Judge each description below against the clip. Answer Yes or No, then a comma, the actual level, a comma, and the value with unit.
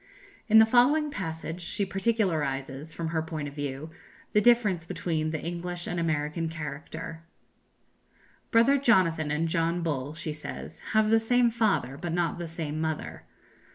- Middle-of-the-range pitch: Yes, medium, 165 Hz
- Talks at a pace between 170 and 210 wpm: No, average, 155 wpm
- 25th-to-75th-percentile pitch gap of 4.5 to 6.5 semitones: Yes, average, 5.2 semitones